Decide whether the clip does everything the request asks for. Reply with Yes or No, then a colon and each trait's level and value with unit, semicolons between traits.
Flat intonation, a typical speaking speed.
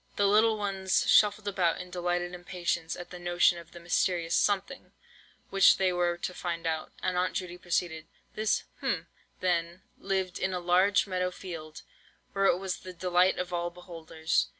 Yes: narrow, 1.7 semitones; average, 165 wpm